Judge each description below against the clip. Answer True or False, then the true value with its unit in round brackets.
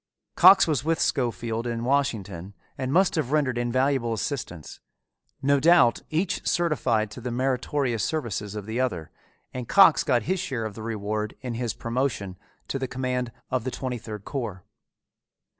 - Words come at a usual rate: True (160 wpm)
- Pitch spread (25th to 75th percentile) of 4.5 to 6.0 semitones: False (4.0 semitones)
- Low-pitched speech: True (125 Hz)